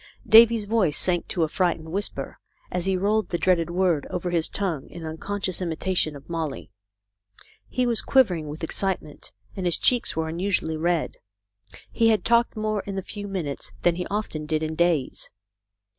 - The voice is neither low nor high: Yes, medium, 175 Hz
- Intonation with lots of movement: No, average, 4.1 semitones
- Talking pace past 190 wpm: No, average, 175 wpm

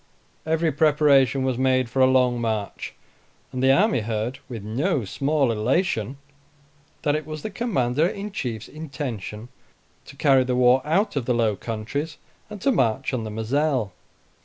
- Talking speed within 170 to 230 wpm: No, average, 160 wpm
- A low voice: Yes, low, 130 Hz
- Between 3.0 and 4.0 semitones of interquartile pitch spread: No, average, 4.7 semitones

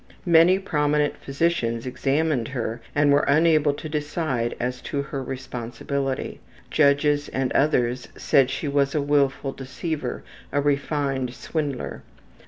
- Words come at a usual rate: No, slow, 125 wpm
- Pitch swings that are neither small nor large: No, narrow, 2.3 semitones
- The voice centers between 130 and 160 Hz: Yes, medium, 140 Hz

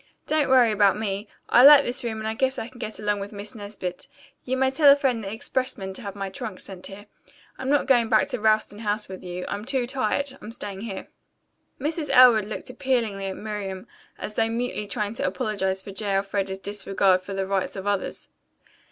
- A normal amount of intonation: Yes, average, 4.1 semitones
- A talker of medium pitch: No, high, 215 Hz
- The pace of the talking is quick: Yes, fast, 210 wpm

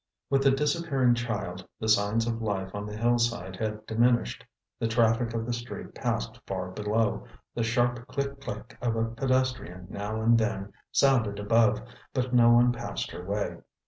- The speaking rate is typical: Yes, average, 170 wpm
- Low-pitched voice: Yes, low, 115 Hz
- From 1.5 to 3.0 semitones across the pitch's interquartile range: Yes, average, 2.7 semitones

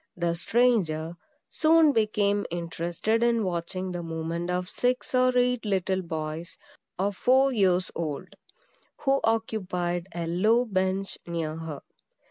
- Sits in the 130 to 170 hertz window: No, medium, 185 Hz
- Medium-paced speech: No, slow, 125 wpm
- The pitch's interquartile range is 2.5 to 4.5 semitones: No, average, 5.0 semitones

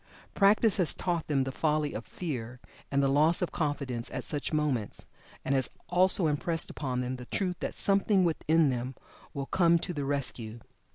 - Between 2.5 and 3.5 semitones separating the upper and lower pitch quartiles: No, average, 4.7 semitones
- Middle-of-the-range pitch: Yes, medium, 150 Hz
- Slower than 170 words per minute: No, average, 175 wpm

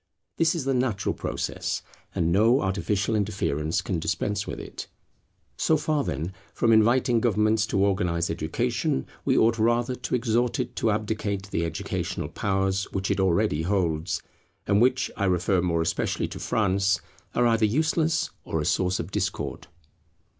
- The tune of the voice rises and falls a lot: No, average, 4.3 semitones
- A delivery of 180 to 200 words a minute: No, average, 155 wpm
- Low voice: Yes, low, 100 Hz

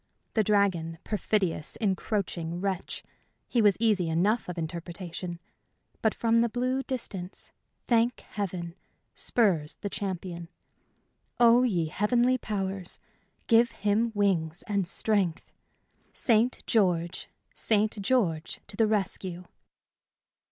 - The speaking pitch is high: Yes, high, 200 Hz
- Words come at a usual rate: No, slow, 110 wpm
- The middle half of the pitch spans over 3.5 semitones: Yes, average, 4.3 semitones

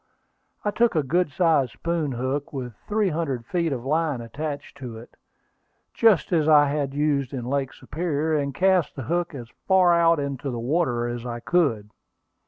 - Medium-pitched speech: Yes, medium, 145 Hz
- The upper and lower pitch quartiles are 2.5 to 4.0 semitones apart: No, average, 4.6 semitones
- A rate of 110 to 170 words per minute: No, average, 185 wpm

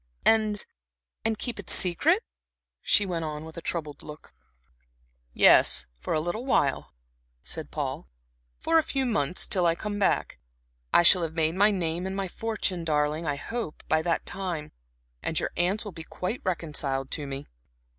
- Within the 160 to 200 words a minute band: Yes, average, 170 wpm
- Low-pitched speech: No, medium, 175 Hz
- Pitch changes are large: No, average, 4.8 semitones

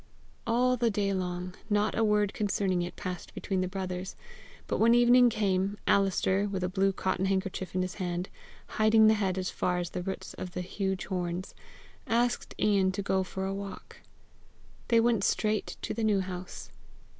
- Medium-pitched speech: No, high, 195 Hz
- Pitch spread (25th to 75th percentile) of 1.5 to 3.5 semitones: Yes, narrow, 2.4 semitones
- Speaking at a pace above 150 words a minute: Yes, average, 180 wpm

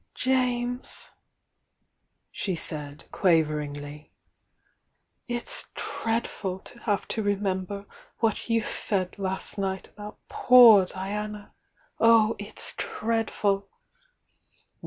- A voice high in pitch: Yes, high, 205 Hz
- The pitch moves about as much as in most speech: Yes, average, 3.3 semitones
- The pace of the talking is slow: Yes, slow, 85 wpm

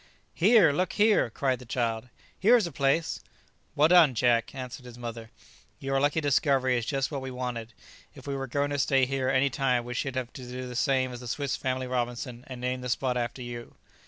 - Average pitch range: No, narrow, 2.2 semitones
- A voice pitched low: Yes, low, 130 Hz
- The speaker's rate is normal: No, fast, 215 wpm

